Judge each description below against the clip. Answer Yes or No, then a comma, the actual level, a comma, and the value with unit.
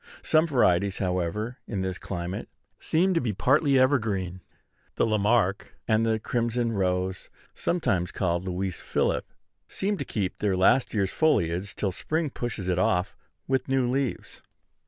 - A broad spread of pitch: Yes, wide, 5.7 semitones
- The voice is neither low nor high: No, low, 105 Hz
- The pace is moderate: Yes, average, 150 wpm